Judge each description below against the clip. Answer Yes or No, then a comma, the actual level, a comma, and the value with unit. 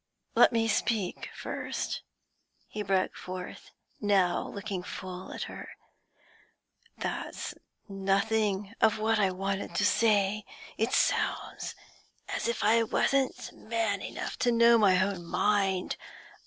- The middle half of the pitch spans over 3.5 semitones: No, narrow, 2.5 semitones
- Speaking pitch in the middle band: No, high, 205 Hz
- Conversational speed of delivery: No, slow, 120 wpm